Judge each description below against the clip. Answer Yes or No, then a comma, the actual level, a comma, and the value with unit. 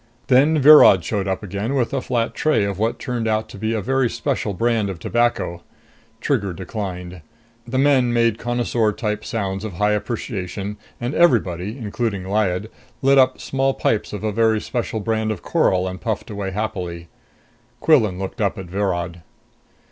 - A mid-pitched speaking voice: No, low, 110 Hz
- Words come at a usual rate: Yes, average, 170 wpm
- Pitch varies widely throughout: No, average, 3.8 semitones